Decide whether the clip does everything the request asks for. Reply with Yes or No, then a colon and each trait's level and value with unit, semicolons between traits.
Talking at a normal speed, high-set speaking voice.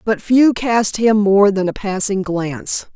Yes: average, 185 wpm; high, 205 Hz